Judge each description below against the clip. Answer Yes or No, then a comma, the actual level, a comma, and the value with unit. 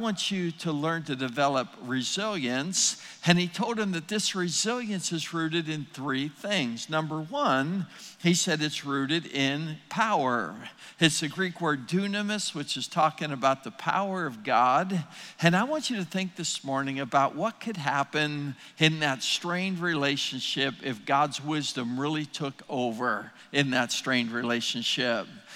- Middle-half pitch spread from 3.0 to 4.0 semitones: No, average, 4.9 semitones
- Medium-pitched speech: Yes, medium, 155 Hz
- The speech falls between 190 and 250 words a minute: No, average, 155 wpm